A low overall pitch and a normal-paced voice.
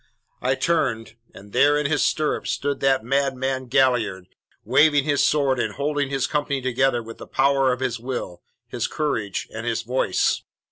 Yes: low, 130 Hz; average, 170 wpm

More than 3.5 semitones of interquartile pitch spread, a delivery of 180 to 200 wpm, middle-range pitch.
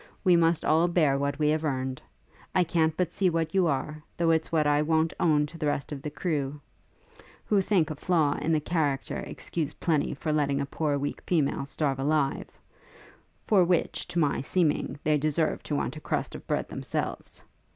No: narrow, 2.5 semitones; average, 195 wpm; medium, 155 Hz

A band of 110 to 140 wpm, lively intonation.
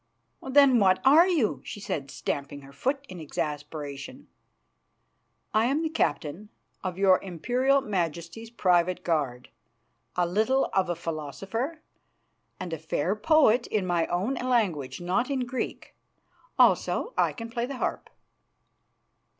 Yes: slow, 135 wpm; wide, 7.3 semitones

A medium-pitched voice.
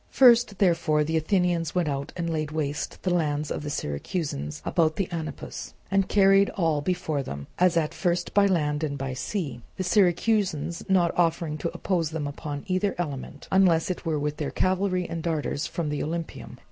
Yes: medium, 165 Hz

